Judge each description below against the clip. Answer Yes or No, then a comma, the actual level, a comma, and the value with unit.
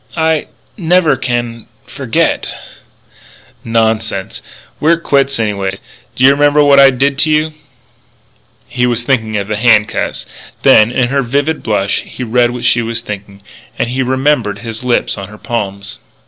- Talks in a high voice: No, low, 120 Hz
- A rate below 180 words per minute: Yes, average, 155 wpm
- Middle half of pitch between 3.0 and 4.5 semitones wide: Yes, average, 4.0 semitones